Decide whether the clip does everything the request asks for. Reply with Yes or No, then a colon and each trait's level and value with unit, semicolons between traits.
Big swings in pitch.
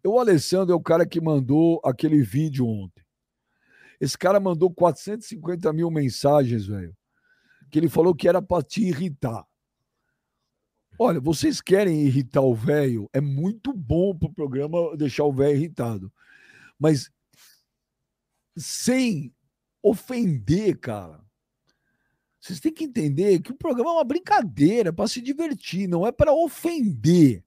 Yes: wide, 6.3 semitones